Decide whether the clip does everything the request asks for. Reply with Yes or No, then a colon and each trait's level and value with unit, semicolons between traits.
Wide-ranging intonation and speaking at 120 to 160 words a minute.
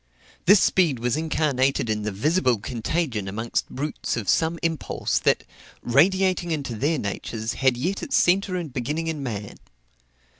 Yes: wide, 6.1 semitones; average, 150 wpm